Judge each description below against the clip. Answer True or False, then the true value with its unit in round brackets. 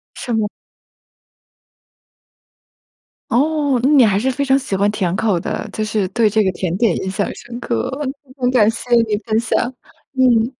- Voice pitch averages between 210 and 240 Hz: True (225 Hz)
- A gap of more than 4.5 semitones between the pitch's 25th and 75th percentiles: False (3.9 semitones)